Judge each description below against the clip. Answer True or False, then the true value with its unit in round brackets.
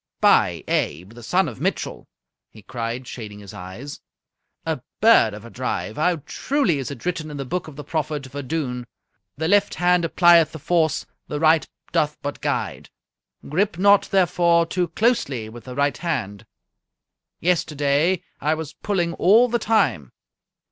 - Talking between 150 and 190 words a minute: True (160 wpm)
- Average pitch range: False (5.7 semitones)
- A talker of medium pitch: True (155 Hz)